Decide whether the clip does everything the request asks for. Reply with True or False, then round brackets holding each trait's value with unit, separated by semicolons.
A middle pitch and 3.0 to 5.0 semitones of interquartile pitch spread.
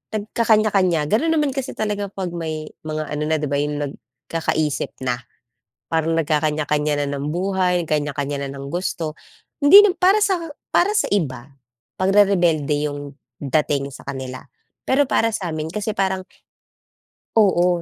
False (165 Hz; 5.5 semitones)